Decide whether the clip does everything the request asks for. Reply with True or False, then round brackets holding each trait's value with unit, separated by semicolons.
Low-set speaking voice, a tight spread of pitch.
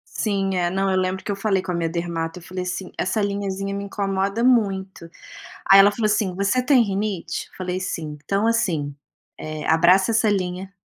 False (195 Hz; 2.0 semitones)